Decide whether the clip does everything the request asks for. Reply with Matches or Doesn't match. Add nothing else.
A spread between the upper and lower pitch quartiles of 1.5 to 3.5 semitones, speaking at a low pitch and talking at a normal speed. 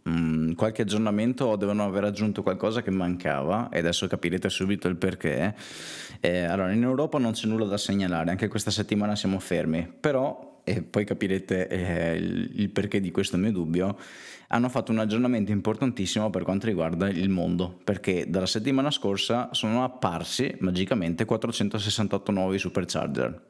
Matches